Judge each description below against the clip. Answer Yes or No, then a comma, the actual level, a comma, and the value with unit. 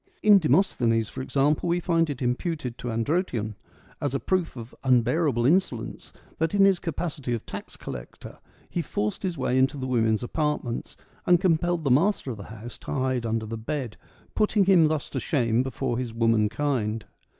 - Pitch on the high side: No, low, 130 Hz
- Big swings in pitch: Yes, wide, 6.1 semitones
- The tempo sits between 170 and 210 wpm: Yes, average, 175 wpm